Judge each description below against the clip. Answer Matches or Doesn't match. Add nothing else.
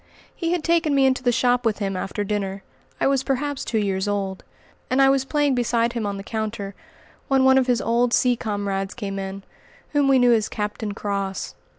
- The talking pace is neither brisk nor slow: Doesn't match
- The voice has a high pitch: Matches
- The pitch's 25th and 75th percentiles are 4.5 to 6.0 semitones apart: Matches